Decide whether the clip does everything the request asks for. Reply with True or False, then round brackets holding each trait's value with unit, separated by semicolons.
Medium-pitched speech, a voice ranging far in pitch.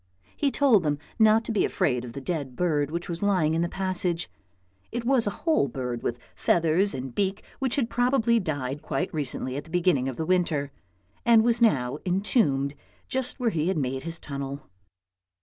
True (170 Hz; 7.5 semitones)